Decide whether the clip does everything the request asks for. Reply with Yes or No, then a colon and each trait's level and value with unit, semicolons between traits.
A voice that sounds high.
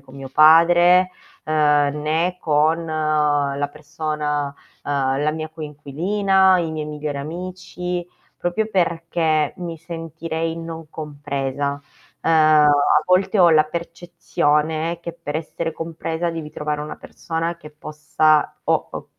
No: medium, 155 Hz